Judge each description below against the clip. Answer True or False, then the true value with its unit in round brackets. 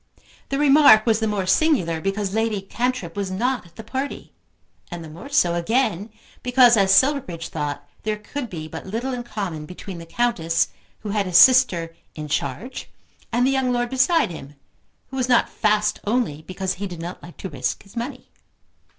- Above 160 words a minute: True (185 wpm)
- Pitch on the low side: False (210 Hz)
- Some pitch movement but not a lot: False (6.4 semitones)